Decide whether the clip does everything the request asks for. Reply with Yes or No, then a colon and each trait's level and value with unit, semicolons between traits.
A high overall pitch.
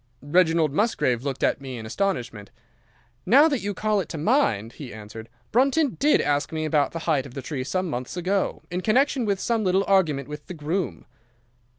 No: medium, 165 Hz